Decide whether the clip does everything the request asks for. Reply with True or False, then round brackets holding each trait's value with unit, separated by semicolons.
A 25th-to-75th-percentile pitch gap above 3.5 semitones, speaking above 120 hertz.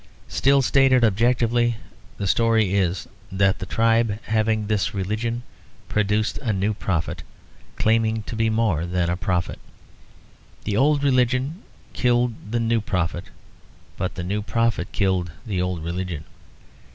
False (3.9 semitones; 110 Hz)